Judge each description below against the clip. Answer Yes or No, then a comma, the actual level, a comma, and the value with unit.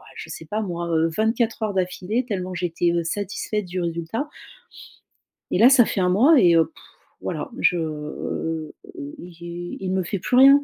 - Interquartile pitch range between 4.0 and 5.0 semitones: Yes, average, 4.6 semitones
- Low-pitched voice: No, medium, 185 Hz